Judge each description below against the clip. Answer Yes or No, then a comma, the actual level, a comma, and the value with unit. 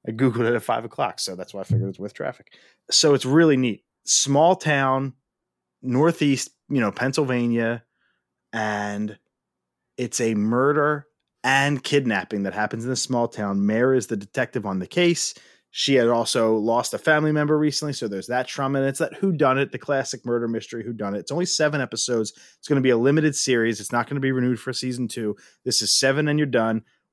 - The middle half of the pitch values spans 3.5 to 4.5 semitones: Yes, average, 3.9 semitones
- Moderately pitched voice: No, low, 125 Hz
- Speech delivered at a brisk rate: Yes, fast, 210 wpm